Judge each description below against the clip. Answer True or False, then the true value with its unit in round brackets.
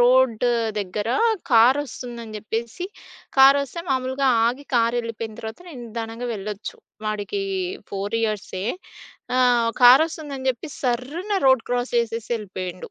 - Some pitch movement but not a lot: True (3.0 semitones)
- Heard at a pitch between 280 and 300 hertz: False (235 Hz)